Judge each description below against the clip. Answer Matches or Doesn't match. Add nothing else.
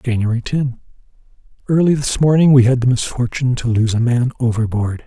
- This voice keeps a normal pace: Matches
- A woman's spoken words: Doesn't match